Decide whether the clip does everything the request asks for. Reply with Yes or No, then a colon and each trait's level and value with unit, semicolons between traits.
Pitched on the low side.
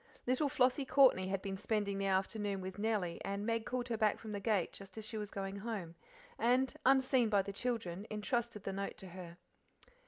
No: high, 210 Hz